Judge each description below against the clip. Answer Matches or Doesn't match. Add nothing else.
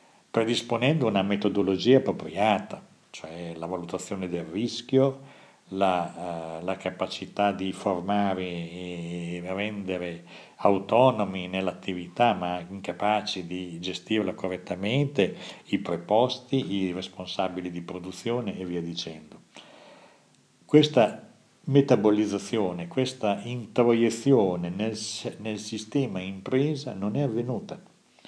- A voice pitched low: Matches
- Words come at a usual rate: Doesn't match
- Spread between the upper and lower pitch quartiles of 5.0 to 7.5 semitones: Doesn't match